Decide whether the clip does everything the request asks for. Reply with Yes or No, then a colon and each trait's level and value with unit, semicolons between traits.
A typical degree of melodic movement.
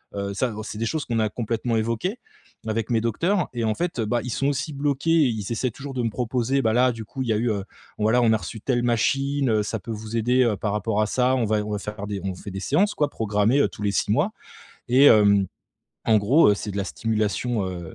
Yes: average, 3.2 semitones